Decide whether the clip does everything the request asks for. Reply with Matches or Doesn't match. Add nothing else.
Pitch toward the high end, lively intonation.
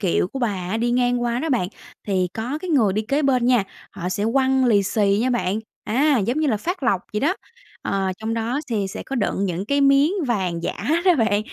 Doesn't match